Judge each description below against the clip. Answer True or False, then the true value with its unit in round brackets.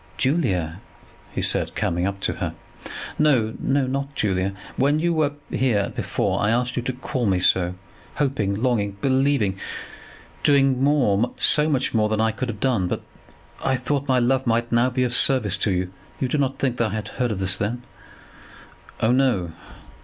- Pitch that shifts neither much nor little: True (4.7 semitones)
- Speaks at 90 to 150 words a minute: False (185 wpm)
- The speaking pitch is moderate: False (120 Hz)